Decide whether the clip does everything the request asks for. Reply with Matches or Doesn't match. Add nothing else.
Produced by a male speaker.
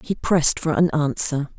Doesn't match